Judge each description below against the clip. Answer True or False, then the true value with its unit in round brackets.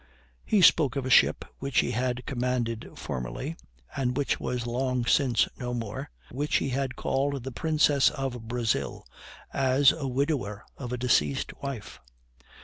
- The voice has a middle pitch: False (125 Hz)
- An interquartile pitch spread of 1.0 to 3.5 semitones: True (2.4 semitones)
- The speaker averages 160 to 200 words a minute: False (150 wpm)